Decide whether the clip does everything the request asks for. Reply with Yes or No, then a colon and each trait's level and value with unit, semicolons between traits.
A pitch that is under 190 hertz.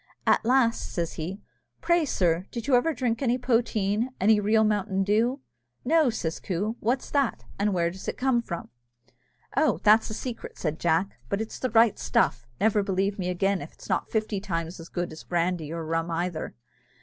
No: high, 205 Hz